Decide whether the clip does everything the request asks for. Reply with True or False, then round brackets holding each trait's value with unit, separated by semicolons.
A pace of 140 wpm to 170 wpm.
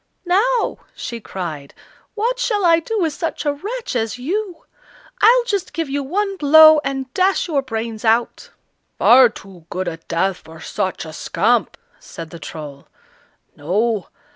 True (155 wpm)